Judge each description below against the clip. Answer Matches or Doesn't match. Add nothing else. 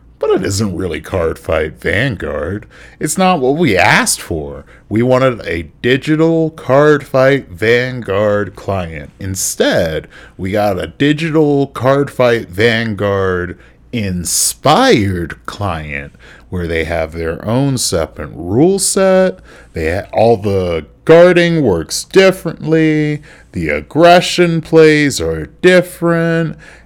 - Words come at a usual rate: Doesn't match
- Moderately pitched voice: Doesn't match